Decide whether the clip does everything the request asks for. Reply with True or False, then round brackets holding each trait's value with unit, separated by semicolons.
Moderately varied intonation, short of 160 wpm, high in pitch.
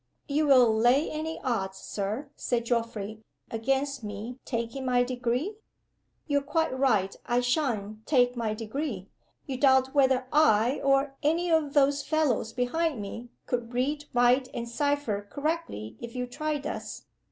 True (3.8 semitones; 145 wpm; 255 Hz)